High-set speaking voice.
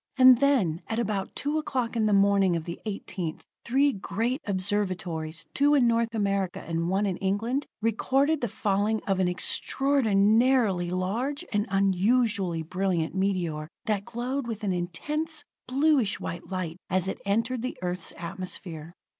Yes: high, 200 Hz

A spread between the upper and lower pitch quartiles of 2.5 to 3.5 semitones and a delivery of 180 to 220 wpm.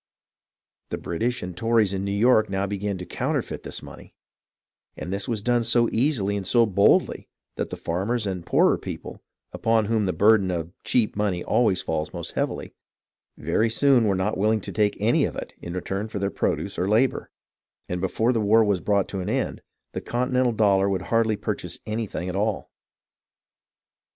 Yes: average, 2.9 semitones; average, 190 wpm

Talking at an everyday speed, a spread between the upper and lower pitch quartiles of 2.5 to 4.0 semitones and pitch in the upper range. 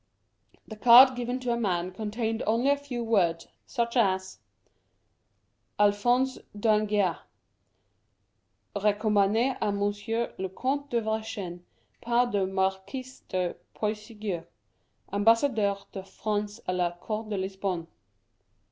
No: slow, 110 wpm; average, 3.5 semitones; high, 210 Hz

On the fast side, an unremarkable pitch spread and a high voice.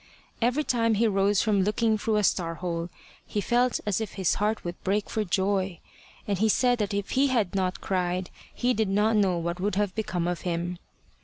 Yes: fast, 210 wpm; average, 3.3 semitones; high, 200 Hz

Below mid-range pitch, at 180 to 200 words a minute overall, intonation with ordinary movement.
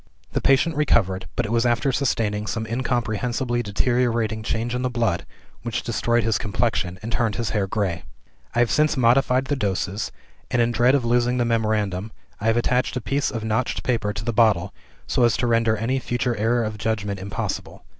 No: low, 115 Hz; average, 195 wpm; narrow, 2.3 semitones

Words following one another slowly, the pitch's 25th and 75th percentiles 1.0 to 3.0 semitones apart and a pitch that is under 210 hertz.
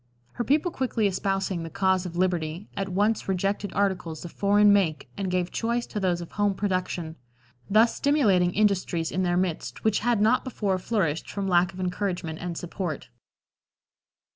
No: average, 165 wpm; average, 2.7 semitones; high, 190 Hz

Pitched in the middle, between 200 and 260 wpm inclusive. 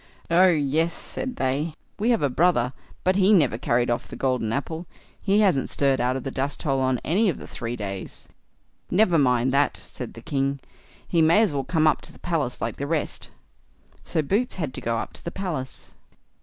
Yes: medium, 145 Hz; fast, 205 wpm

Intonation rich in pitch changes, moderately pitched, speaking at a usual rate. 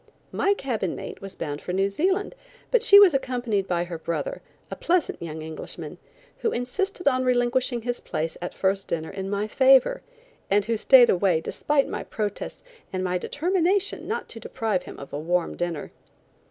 No: wide, 7.9 semitones; high, 225 Hz; average, 180 wpm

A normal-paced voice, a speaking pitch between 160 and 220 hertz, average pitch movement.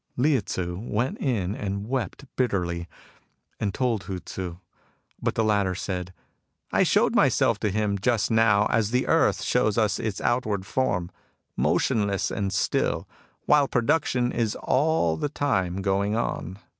No: average, 150 wpm; low, 105 Hz; average, 4.1 semitones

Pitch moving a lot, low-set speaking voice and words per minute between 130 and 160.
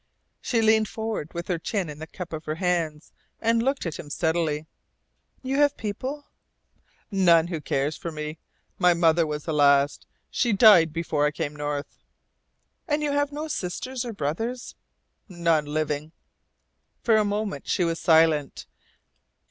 No: wide, 6.3 semitones; medium, 170 Hz; average, 155 wpm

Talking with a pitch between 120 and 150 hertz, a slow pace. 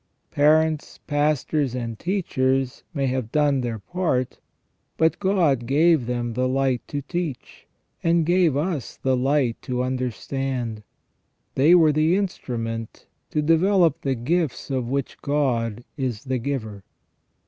Yes: low, 135 Hz; slow, 130 wpm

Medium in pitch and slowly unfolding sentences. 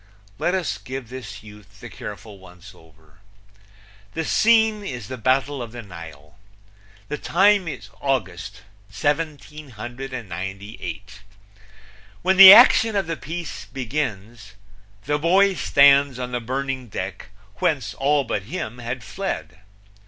No: low, 130 Hz; slow, 125 wpm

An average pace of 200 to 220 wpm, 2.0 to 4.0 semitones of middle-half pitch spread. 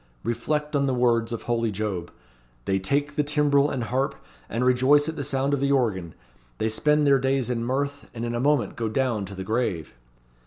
Yes: fast, 205 wpm; average, 3.7 semitones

